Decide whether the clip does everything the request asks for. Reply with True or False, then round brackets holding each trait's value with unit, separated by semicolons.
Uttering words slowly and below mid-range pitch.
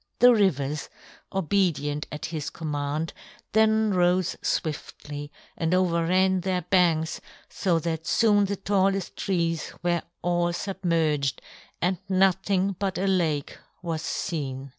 False (120 wpm; 175 Hz)